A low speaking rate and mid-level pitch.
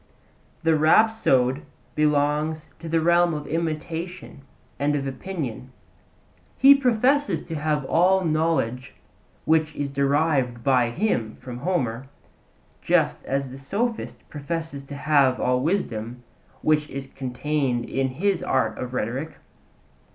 Yes: slow, 120 wpm; medium, 150 Hz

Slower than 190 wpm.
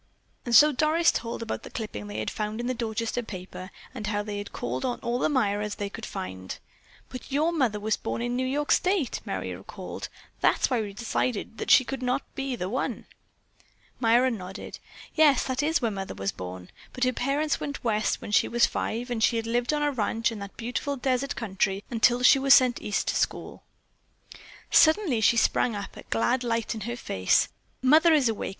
No: fast, 205 wpm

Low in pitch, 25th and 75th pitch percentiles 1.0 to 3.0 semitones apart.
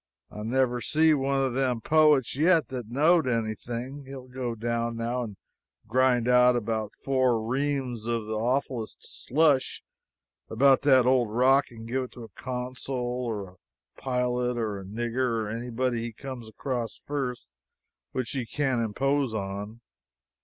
Yes: low, 125 Hz; narrow, 2.4 semitones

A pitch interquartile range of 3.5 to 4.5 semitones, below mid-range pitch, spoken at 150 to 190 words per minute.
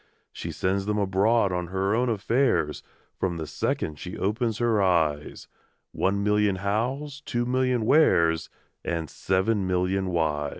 No: average, 4.2 semitones; low, 100 Hz; average, 140 wpm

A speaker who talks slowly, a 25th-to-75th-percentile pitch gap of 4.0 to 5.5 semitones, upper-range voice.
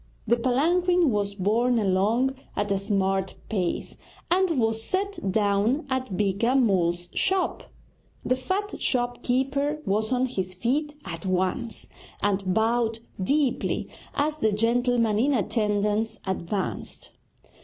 Yes: slow, 125 wpm; average, 4.6 semitones; high, 225 Hz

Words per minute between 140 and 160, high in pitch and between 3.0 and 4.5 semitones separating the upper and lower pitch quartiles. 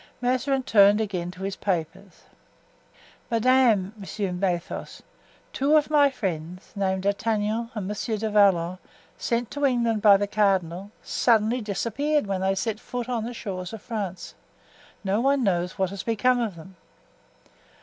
Yes: average, 150 wpm; high, 210 Hz; average, 3.8 semitones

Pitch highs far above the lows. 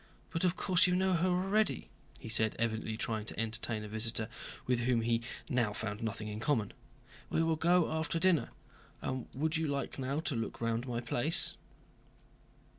Yes: wide, 6.5 semitones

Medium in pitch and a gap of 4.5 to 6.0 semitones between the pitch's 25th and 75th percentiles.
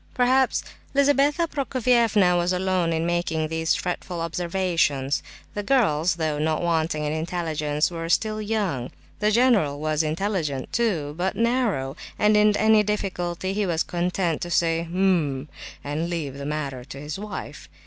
Yes: medium, 175 Hz; average, 5.2 semitones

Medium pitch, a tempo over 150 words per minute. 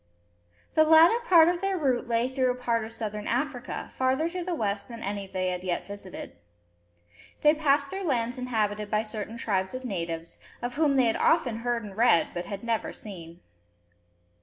No: high, 235 Hz; average, 185 wpm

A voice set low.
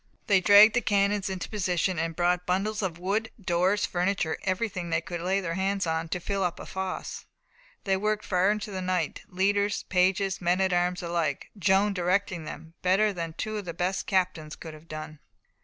No: medium, 185 Hz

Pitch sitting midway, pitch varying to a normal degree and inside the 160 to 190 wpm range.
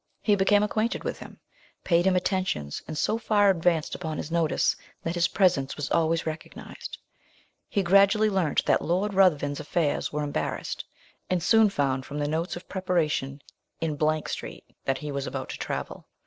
Yes: medium, 170 Hz; average, 4.5 semitones; average, 170 wpm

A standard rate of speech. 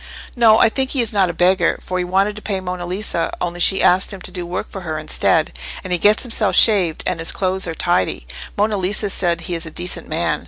No: fast, 245 wpm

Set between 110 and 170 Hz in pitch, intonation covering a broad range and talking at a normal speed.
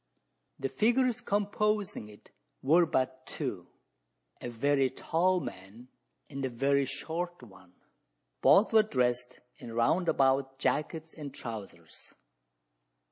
No: low, 135 Hz; wide, 6.3 semitones; slow, 115 wpm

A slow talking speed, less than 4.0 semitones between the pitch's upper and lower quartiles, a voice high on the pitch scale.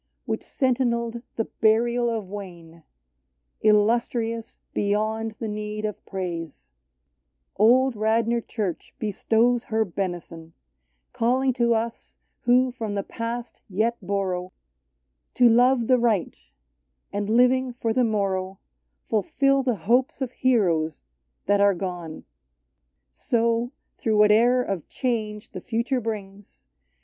Yes: slow, 120 wpm; average, 3.4 semitones; high, 220 Hz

